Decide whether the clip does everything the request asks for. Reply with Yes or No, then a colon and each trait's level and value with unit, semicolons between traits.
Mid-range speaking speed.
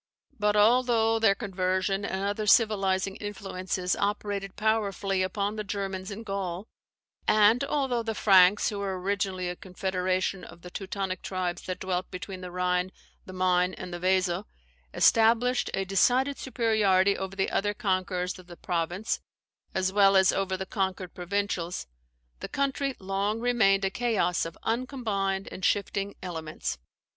Yes: average, 150 wpm